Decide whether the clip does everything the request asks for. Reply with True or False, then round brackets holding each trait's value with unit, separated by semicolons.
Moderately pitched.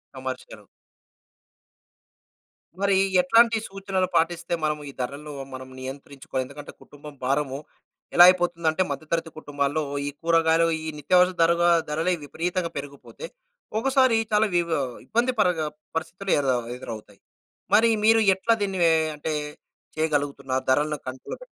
True (160 Hz)